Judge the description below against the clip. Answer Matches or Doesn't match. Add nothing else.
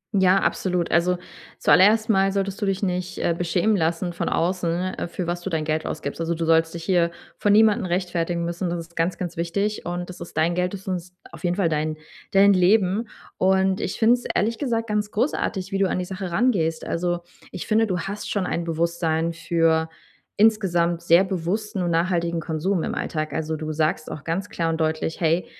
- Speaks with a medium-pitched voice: Matches